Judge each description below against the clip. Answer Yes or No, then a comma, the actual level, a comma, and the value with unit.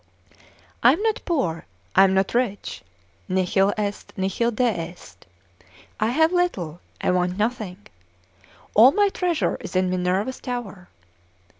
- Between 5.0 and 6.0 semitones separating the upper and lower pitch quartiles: Yes, wide, 5.4 semitones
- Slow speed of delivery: Yes, slow, 130 wpm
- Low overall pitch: No, high, 205 Hz